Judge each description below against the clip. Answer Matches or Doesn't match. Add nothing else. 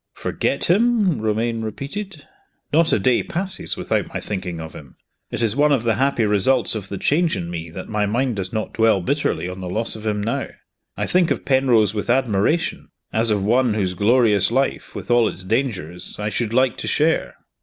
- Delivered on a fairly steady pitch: Doesn't match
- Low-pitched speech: Matches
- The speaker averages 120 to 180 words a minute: Doesn't match